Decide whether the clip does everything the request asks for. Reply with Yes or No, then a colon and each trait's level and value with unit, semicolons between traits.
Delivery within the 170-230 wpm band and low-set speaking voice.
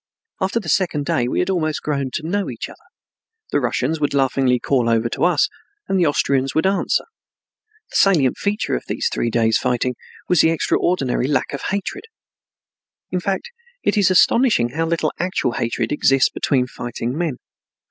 No: average, 175 wpm; medium, 145 Hz